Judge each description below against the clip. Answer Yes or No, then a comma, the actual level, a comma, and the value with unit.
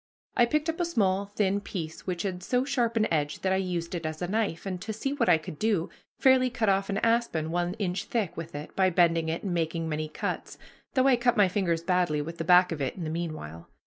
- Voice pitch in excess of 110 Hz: Yes, medium, 185 Hz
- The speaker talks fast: Yes, fast, 250 wpm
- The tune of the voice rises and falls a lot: No, average, 4.9 semitones